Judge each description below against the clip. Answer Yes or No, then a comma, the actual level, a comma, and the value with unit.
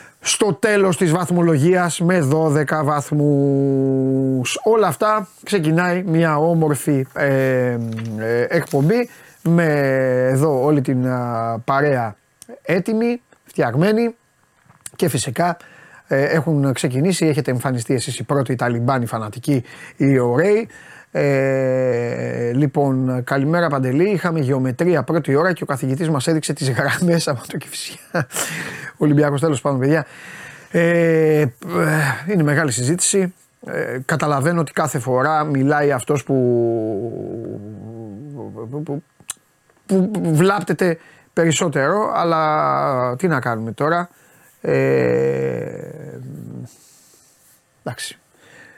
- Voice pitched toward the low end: No, medium, 145 Hz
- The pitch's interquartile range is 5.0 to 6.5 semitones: No, average, 4.2 semitones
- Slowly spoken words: Yes, slow, 100 wpm